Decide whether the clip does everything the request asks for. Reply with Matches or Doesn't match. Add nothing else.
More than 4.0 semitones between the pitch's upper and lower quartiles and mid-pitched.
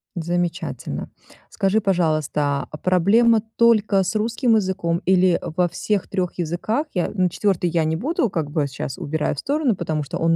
Matches